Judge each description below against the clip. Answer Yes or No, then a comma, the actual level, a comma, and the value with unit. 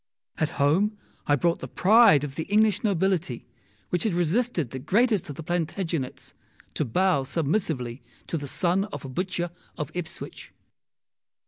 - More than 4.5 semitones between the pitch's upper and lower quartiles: Yes, average, 5.1 semitones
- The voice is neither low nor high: Yes, medium, 170 Hz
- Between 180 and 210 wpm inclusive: No, average, 150 wpm